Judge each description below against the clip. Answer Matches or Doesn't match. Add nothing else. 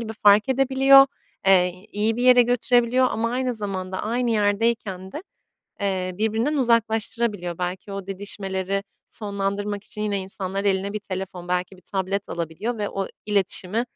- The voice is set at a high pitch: Matches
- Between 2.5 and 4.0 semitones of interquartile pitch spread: Matches